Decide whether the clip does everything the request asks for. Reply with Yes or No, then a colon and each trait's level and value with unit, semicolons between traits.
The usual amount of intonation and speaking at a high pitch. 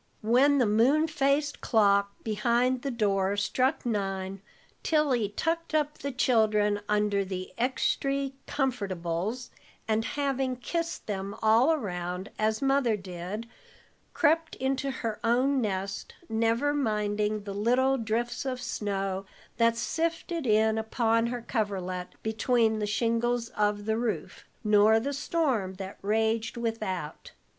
Yes: average, 4.2 semitones; high, 225 Hz